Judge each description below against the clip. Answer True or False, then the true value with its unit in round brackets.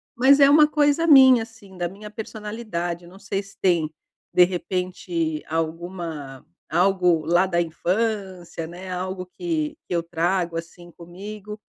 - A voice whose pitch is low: False (185 Hz)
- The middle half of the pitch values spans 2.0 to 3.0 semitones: False (3.8 semitones)